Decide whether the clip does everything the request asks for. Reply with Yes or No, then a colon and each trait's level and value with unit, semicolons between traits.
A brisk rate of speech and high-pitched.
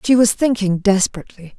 No: average, 150 wpm; high, 205 Hz